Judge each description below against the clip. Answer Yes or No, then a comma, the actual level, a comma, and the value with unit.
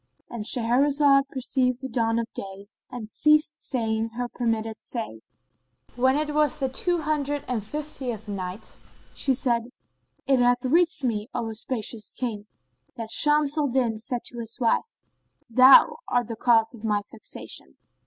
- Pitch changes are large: No, average, 3.6 semitones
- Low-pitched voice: No, high, 245 Hz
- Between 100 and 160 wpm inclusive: Yes, average, 155 wpm